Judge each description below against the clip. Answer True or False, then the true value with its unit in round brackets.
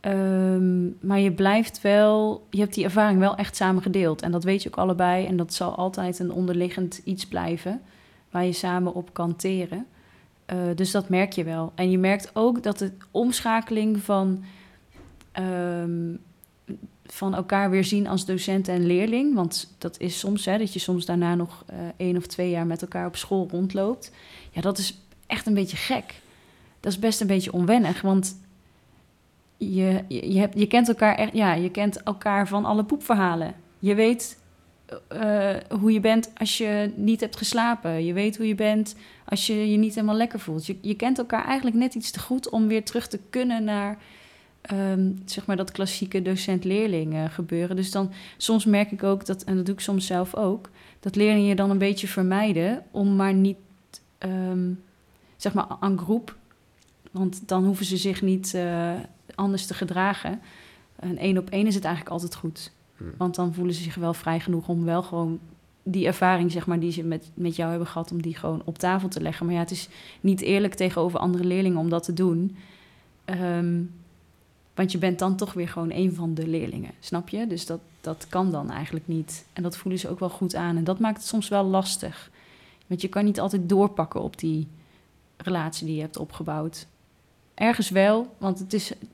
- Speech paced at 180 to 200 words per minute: True (195 wpm)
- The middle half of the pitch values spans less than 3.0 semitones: True (2.6 semitones)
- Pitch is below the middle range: False (190 Hz)